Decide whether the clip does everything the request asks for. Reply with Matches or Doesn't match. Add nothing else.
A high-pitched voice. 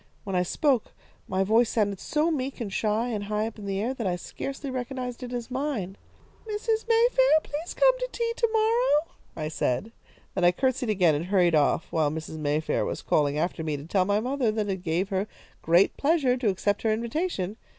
Matches